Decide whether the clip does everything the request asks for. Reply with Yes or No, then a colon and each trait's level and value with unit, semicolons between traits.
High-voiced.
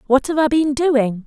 Yes: very high, 275 Hz